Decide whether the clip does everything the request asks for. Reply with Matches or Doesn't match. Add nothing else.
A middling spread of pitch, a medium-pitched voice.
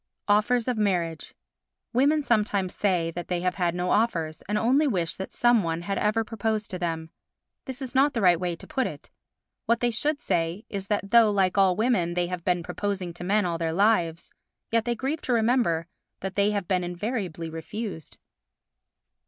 Doesn't match